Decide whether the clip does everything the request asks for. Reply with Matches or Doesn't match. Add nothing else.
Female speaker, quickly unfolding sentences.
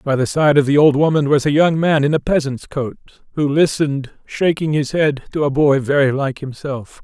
Doesn't match